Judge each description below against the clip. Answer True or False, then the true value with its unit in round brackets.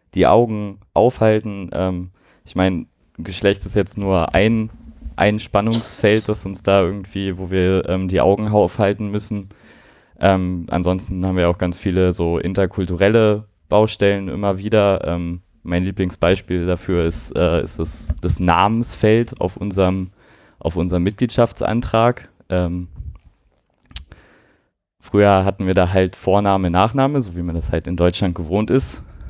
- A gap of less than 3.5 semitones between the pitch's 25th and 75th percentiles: True (2.7 semitones)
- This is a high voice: False (95 Hz)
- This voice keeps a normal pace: True (140 wpm)